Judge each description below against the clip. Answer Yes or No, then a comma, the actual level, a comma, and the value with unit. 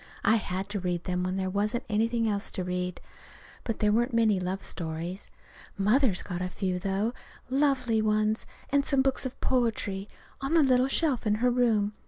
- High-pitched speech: Yes, high, 215 Hz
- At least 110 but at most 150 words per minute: No, average, 185 wpm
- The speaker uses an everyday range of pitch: Yes, average, 4.4 semitones